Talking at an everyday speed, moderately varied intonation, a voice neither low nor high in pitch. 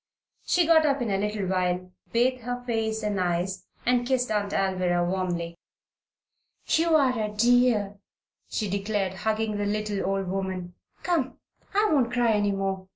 No: average, 160 wpm; average, 4.2 semitones; high, 210 Hz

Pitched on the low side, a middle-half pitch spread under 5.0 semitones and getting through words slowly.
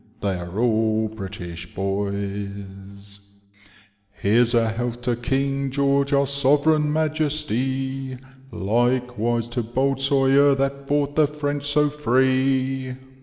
Yes: low, 130 Hz; average, 4.3 semitones; slow, 115 wpm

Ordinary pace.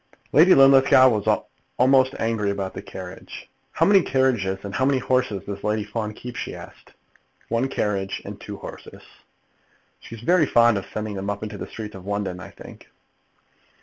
Yes: average, 175 wpm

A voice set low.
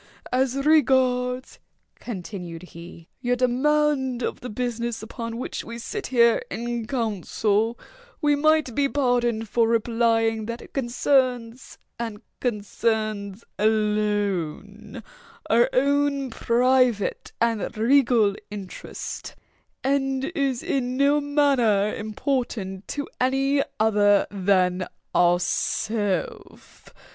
No: high, 235 Hz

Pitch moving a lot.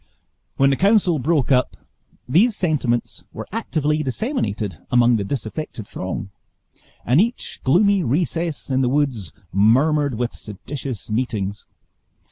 Yes: wide, 5.7 semitones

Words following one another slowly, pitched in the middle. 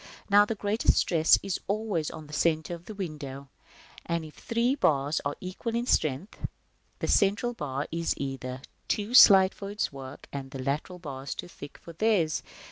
No: average, 195 wpm; medium, 170 Hz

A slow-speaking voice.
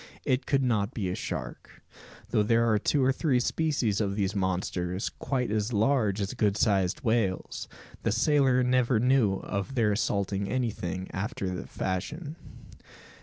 No: average, 155 wpm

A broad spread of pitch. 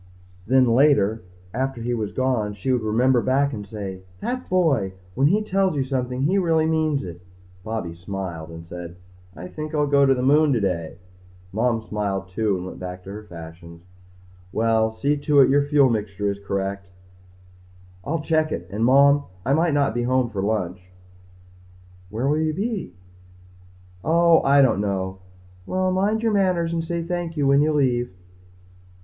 Yes: wide, 7.1 semitones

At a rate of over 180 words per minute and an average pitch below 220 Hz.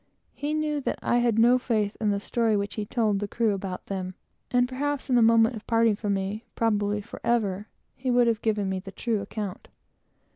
No: average, 195 wpm; high, 225 Hz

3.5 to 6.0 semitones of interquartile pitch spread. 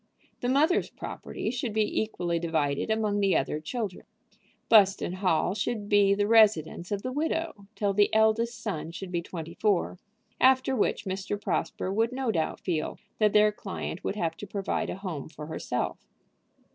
Yes: average, 3.9 semitones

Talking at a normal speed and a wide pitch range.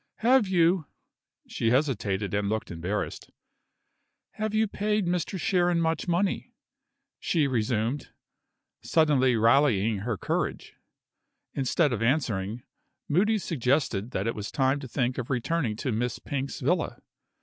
No: slow, 130 wpm; wide, 7.0 semitones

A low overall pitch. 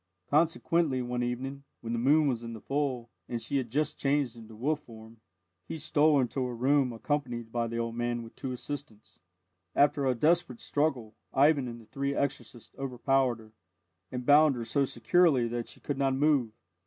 Yes: low, 130 Hz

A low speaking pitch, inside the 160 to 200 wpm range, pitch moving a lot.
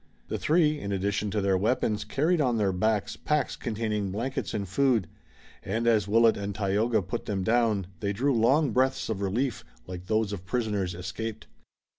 No: low, 110 Hz; average, 175 wpm; average, 3.4 semitones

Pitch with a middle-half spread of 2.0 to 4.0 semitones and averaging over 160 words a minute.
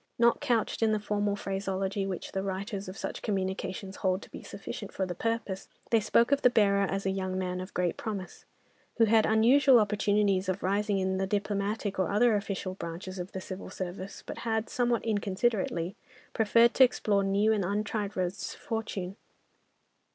Yes: narrow, 2.4 semitones; average, 180 wpm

